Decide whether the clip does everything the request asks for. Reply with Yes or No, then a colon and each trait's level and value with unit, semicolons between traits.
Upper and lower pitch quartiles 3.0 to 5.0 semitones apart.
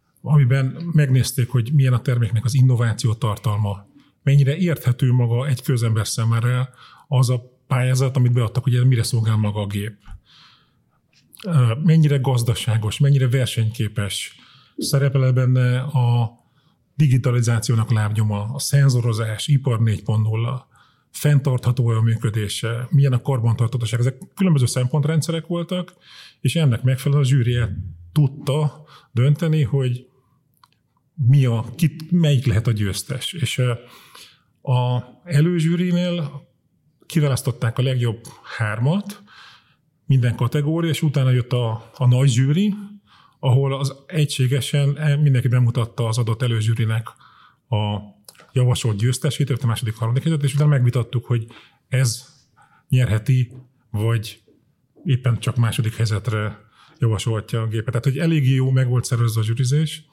Yes: average, 3.3 semitones